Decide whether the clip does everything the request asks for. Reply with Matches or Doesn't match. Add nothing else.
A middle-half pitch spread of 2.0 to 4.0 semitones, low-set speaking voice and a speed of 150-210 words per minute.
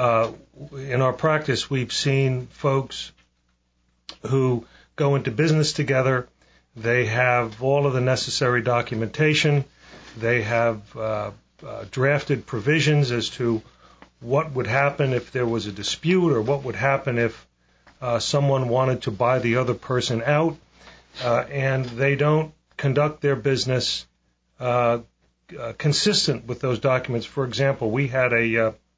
Doesn't match